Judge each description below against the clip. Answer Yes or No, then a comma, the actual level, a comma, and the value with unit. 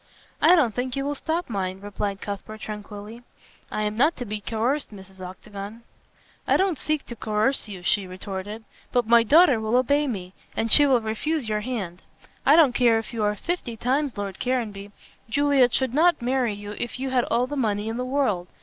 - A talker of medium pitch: No, high, 230 Hz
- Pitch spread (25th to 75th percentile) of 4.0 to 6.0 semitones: Yes, average, 4.4 semitones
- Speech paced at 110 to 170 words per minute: No, average, 200 wpm